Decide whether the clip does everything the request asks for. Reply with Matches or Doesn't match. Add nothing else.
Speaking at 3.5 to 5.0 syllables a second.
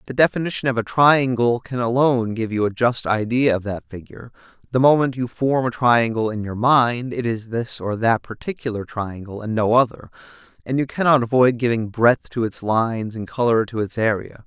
Doesn't match